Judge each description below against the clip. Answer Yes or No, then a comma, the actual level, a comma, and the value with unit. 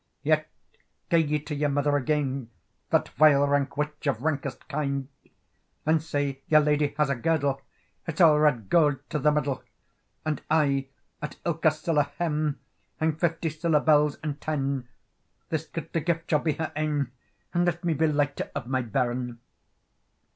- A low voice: No, medium, 150 Hz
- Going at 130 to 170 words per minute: Yes, average, 160 wpm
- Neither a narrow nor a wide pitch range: No, narrow, 2.0 semitones